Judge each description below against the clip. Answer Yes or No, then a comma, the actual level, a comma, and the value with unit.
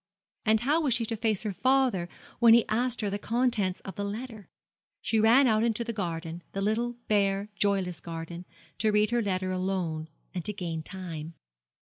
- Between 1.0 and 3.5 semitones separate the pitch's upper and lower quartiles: No, average, 3.9 semitones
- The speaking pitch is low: No, high, 205 Hz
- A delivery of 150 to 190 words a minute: Yes, average, 185 wpm